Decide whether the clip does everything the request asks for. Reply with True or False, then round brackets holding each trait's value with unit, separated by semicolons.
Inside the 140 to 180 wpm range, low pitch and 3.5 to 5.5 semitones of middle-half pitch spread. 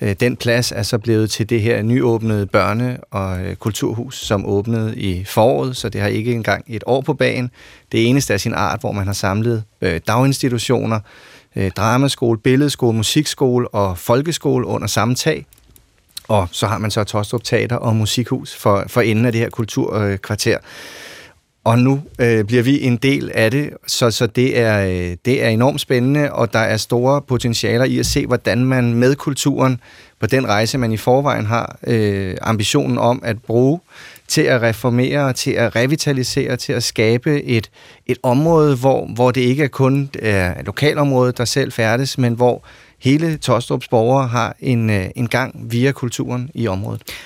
False (175 wpm; 120 Hz; 2.8 semitones)